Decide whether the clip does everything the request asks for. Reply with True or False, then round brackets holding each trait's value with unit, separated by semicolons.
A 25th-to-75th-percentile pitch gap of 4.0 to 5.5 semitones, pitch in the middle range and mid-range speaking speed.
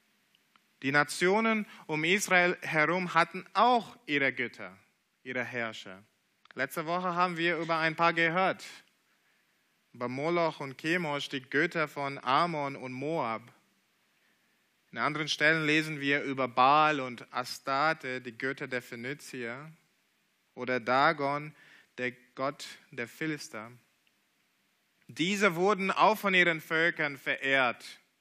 False (4.6 semitones; 150 Hz; 120 wpm)